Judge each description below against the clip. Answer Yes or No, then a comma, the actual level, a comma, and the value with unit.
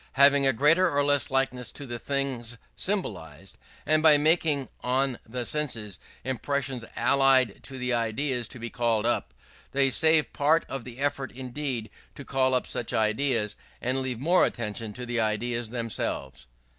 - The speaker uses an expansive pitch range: No, average, 3.3 semitones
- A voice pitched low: Yes, low, 130 Hz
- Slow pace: No, average, 160 wpm